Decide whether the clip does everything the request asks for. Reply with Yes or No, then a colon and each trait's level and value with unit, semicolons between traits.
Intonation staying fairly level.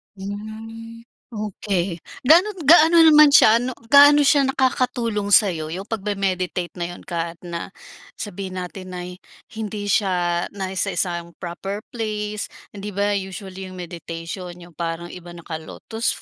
No: average, 4.2 semitones